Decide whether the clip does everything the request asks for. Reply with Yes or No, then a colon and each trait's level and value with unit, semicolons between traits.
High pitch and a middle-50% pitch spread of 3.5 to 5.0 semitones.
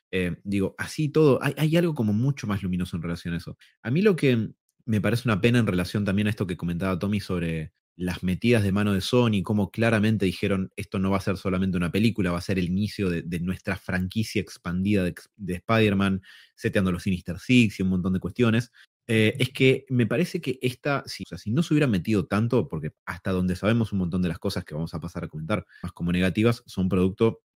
No: low, 100 Hz; average, 4.1 semitones